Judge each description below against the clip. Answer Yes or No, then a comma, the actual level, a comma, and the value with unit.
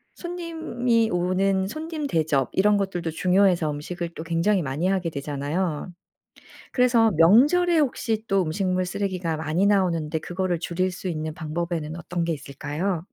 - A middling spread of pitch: Yes, average, 3.9 semitones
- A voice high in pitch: No, medium, 180 Hz